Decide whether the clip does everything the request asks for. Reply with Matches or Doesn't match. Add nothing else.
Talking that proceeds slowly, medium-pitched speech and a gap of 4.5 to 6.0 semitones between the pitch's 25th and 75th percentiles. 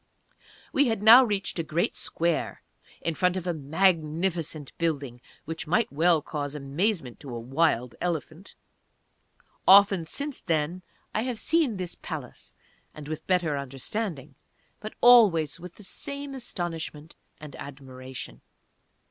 Matches